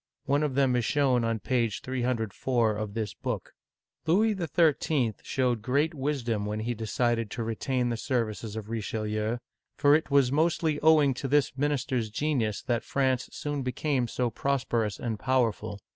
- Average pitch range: Yes, average, 3.9 semitones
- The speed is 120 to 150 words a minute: No, average, 165 wpm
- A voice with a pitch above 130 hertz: No, low, 125 Hz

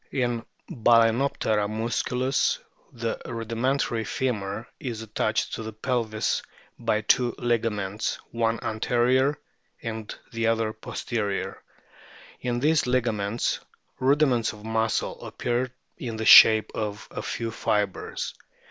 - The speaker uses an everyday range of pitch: No, narrow, 2.0 semitones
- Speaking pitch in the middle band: No, low, 115 Hz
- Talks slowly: Yes, slow, 115 wpm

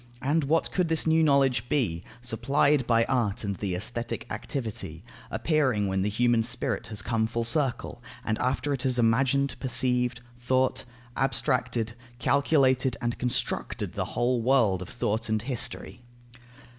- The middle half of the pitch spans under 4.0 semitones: Yes, average, 3.1 semitones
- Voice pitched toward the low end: Yes, low, 125 Hz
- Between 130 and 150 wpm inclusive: Yes, average, 145 wpm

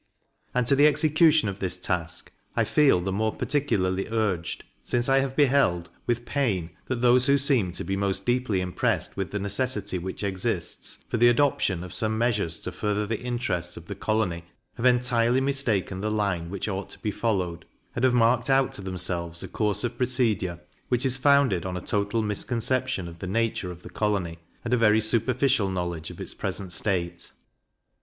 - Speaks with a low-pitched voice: Yes, low, 105 Hz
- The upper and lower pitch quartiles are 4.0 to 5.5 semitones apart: Yes, average, 5.2 semitones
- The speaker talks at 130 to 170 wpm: No, average, 190 wpm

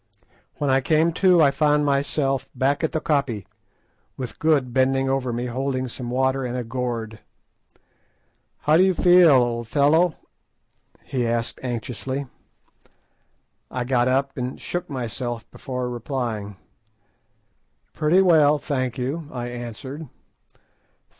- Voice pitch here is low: Yes, low, 130 Hz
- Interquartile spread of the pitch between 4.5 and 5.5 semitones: No, average, 3.3 semitones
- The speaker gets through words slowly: Yes, slow, 125 wpm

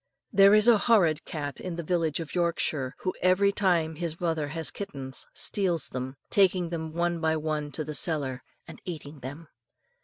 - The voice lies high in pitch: No, medium, 165 Hz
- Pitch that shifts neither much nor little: Yes, average, 3.2 semitones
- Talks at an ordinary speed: Yes, average, 180 wpm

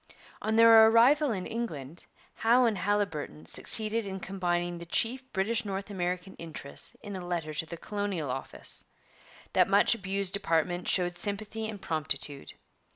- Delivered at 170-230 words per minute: No, average, 150 wpm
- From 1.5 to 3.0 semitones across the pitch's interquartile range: No, average, 4.3 semitones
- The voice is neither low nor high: No, high, 195 Hz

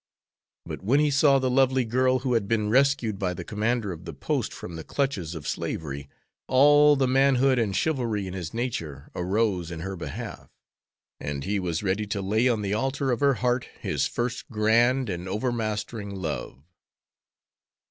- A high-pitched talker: No, low, 110 Hz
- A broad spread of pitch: Yes, wide, 5.7 semitones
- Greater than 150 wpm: Yes, average, 175 wpm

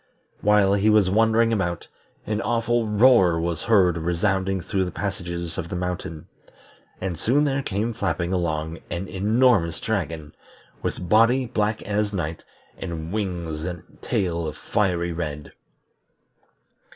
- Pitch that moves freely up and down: No, average, 4.0 semitones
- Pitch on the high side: No, very low, 95 Hz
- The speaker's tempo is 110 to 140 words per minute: Yes, slow, 135 wpm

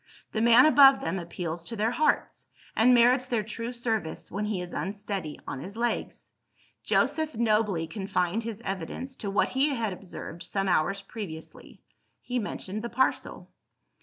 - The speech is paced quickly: No, average, 160 wpm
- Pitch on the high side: Yes, high, 215 Hz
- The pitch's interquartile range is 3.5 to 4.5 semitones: Yes, average, 4.1 semitones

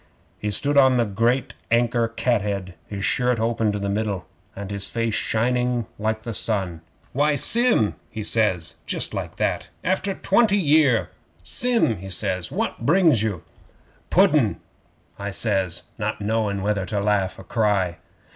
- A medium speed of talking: Yes, average, 150 wpm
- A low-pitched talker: Yes, low, 110 Hz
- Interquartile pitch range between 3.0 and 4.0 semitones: Yes, average, 3.6 semitones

